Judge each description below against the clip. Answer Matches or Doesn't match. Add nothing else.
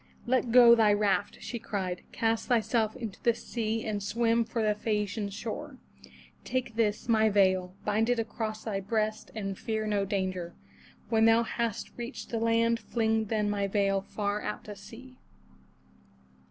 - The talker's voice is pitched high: Matches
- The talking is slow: Doesn't match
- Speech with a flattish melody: Matches